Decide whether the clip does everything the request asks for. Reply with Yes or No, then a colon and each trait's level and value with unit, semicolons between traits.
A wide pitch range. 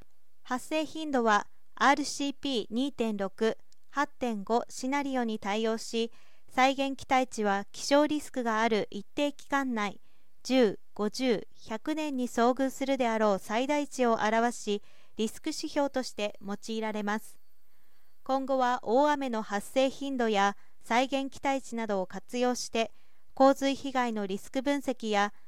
No: average, 3.9 semitones